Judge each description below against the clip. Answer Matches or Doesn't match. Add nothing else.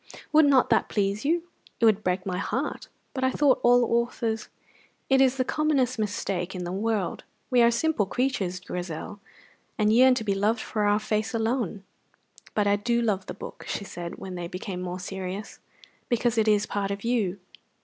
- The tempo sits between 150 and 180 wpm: Doesn't match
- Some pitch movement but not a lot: Matches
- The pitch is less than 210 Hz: Doesn't match